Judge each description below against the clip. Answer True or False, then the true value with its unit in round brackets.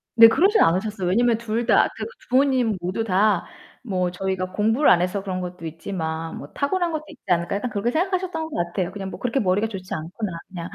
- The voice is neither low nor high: False (200 Hz)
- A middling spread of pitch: True (4.8 semitones)